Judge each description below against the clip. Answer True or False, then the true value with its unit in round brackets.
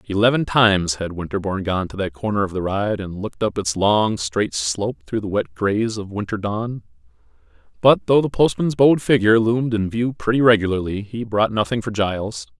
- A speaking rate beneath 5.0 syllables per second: False (5.5 syllables/s)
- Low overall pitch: True (105 Hz)